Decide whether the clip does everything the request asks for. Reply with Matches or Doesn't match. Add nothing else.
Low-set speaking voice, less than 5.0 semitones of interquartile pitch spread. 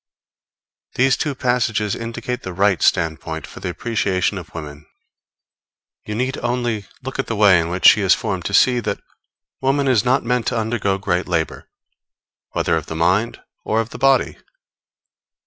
Doesn't match